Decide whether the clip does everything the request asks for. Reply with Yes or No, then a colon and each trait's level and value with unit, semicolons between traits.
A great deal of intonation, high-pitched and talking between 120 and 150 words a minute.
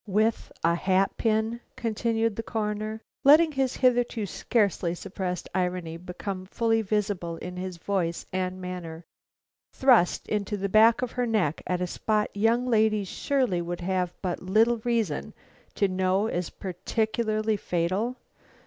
No: average, 3.7 semitones; high, 205 Hz; average, 140 wpm